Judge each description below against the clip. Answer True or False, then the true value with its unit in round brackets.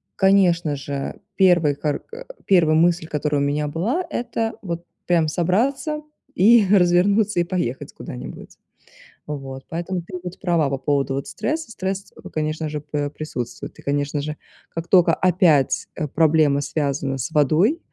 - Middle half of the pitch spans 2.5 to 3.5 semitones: False (4.4 semitones)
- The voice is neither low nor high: True (165 Hz)